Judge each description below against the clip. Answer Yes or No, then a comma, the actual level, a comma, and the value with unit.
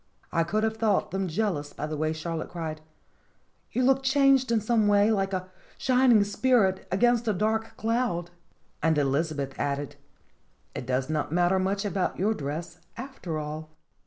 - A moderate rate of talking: Yes, average, 160 wpm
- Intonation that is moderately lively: No, wide, 5.9 semitones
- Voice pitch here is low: No, high, 190 Hz